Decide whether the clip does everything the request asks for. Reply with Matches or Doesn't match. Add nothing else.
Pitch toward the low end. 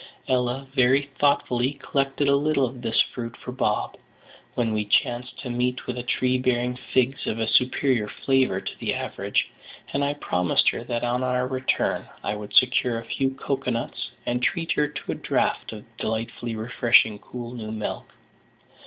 Matches